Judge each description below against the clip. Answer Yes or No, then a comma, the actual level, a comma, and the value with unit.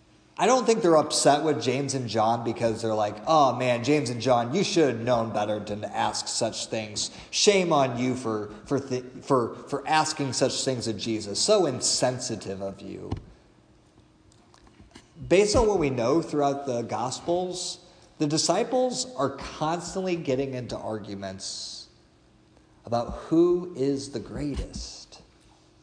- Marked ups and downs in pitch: Yes, wide, 5.8 semitones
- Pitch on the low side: Yes, low, 125 Hz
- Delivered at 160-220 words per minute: No, average, 145 wpm